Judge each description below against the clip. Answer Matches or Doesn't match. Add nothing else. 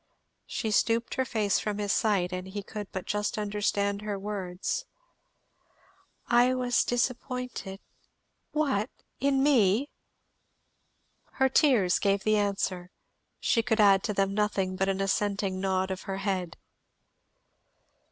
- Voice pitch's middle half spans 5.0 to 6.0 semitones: Doesn't match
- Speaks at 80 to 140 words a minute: Matches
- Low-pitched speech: Doesn't match